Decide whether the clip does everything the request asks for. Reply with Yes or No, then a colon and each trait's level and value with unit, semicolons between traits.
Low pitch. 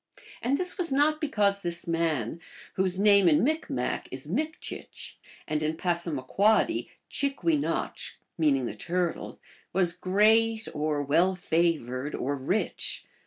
No: medium, 180 Hz